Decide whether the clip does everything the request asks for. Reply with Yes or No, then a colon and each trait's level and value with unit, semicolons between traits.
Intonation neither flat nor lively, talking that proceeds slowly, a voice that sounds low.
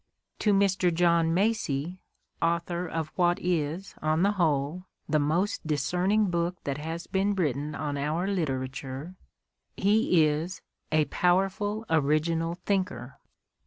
No: average, 3.6 semitones; slow, 125 wpm; medium, 170 Hz